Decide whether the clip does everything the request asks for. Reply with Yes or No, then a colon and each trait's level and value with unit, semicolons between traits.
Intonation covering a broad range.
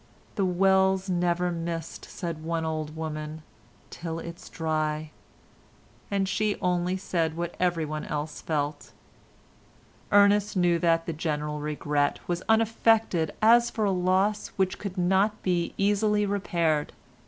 No: average, 3.6 semitones